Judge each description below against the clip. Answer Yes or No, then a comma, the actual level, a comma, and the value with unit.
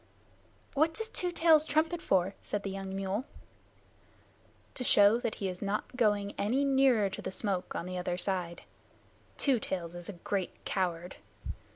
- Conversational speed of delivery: Yes, average, 165 wpm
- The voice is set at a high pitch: Yes, high, 200 Hz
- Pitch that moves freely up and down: Yes, wide, 6.2 semitones